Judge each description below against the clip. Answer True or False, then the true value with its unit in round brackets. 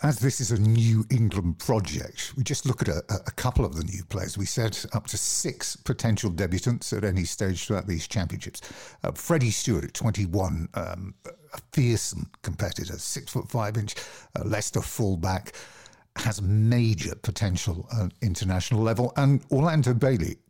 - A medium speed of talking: True (160 wpm)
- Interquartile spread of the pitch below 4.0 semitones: False (4.3 semitones)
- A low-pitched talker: True (110 Hz)